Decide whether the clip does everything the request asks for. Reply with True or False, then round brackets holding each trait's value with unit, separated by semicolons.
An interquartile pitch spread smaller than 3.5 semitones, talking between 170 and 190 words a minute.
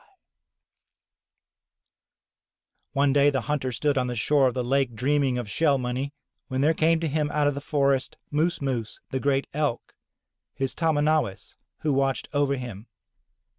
False (2.4 semitones; 160 wpm)